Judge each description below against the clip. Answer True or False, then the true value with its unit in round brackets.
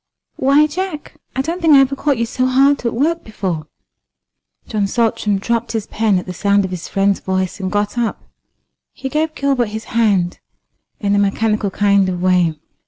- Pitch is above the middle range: True (220 Hz)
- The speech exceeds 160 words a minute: True (185 wpm)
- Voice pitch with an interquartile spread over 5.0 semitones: True (5.5 semitones)